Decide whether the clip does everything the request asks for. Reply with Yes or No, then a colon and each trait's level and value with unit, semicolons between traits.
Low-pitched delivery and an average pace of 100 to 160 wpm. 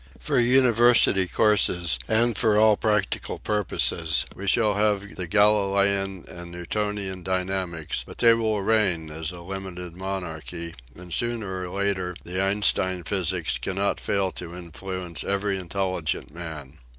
Yes: very low, 95 Hz; average, 140 wpm